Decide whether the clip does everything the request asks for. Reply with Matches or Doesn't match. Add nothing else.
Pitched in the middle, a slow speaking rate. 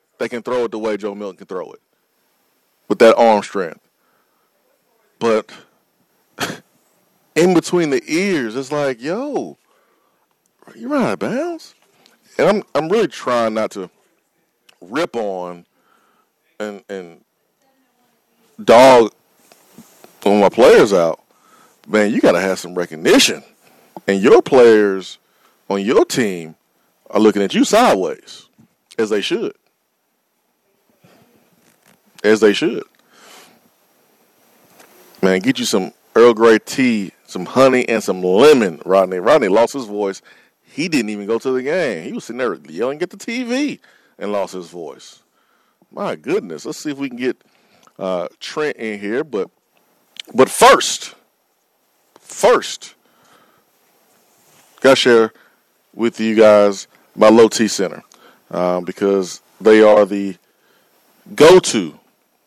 Doesn't match